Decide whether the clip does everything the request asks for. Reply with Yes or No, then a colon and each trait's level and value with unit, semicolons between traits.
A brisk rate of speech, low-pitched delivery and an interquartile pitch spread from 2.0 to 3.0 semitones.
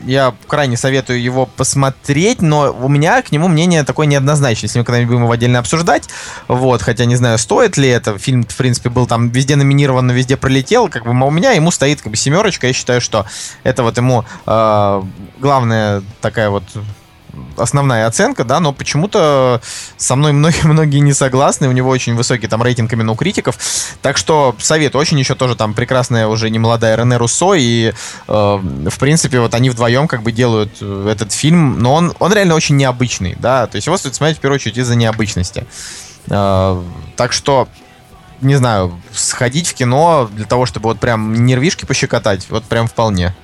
No: fast, 185 wpm; low, 125 Hz; average, 3.8 semitones